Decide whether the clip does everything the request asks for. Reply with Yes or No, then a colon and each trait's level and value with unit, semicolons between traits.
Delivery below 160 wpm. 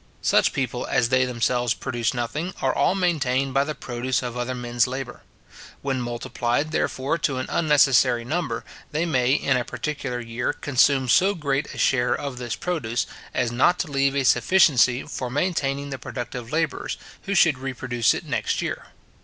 No: average, 170 wpm